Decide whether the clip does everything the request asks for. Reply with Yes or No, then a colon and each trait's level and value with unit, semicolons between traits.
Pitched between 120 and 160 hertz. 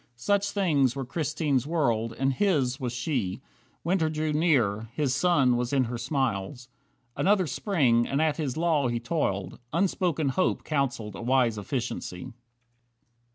Yes: low, 135 Hz